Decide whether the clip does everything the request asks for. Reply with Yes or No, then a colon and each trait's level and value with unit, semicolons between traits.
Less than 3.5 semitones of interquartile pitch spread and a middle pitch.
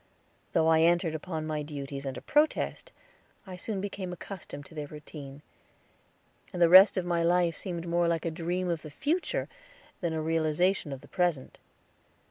Yes: average, 2.7 semitones; medium, 170 Hz